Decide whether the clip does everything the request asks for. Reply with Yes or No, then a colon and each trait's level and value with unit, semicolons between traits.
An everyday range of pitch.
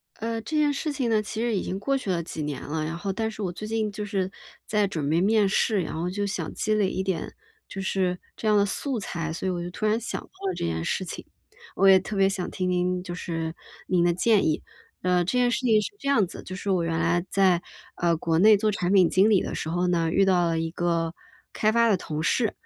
Yes: average, 3.7 semitones